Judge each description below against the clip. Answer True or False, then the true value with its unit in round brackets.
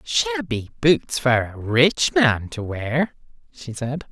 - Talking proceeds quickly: False (145 wpm)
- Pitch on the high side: False (145 Hz)